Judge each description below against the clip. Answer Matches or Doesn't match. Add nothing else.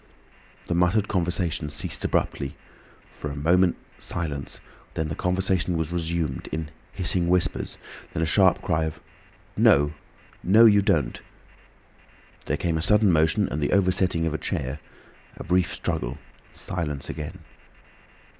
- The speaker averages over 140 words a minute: Doesn't match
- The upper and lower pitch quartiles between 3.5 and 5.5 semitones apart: Doesn't match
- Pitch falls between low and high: Doesn't match